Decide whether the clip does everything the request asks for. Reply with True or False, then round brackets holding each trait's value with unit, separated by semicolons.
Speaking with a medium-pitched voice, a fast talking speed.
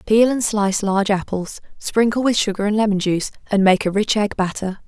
False (205 Hz; 210 wpm)